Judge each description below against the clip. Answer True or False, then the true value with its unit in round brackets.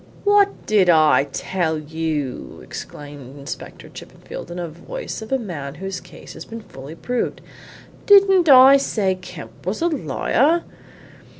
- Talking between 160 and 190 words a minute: False (140 wpm)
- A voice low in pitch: False (180 Hz)